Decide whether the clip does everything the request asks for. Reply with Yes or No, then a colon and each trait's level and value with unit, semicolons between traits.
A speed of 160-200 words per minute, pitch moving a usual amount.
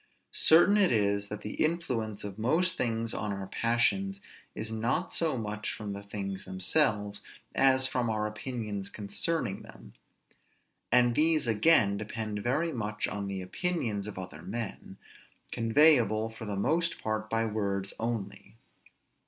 No: average, 145 wpm; average, 4.3 semitones